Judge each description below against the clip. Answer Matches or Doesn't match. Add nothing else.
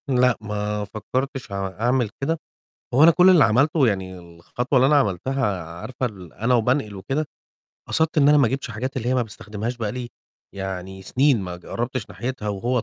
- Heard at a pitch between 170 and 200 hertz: Doesn't match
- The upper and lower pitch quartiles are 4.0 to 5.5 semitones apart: Matches